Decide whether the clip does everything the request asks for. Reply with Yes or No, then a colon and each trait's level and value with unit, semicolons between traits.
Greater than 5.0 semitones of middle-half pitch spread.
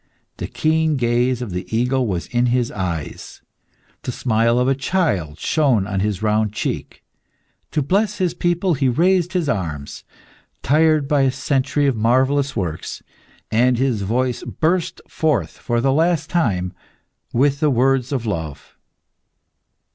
Yes: wide, 5.5 semitones